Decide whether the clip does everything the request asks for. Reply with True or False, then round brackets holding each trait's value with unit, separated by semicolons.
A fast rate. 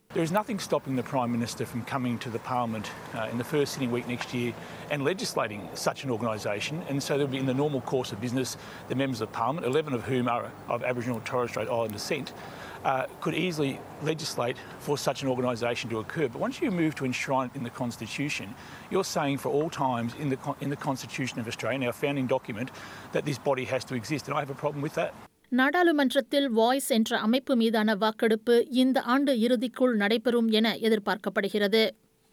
True (200 wpm)